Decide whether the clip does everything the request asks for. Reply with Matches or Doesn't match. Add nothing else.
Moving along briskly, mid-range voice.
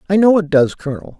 Matches